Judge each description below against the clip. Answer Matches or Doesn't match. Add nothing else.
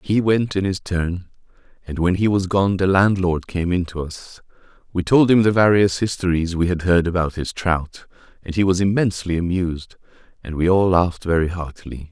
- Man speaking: Matches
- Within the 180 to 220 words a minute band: Matches